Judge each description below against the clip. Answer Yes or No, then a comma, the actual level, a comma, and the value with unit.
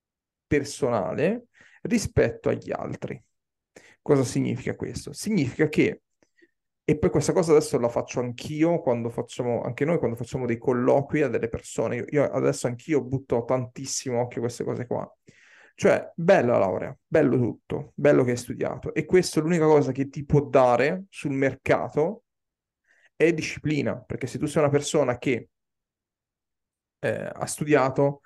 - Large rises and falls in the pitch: No, average, 3.6 semitones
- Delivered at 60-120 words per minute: No, average, 150 wpm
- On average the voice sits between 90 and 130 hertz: No, medium, 140 Hz